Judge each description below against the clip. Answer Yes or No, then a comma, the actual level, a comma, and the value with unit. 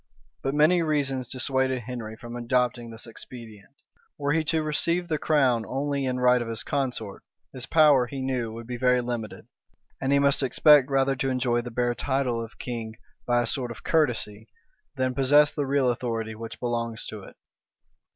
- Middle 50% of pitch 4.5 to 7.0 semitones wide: No, average, 2.8 semitones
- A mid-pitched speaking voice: No, low, 125 Hz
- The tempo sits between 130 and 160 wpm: No, average, 180 wpm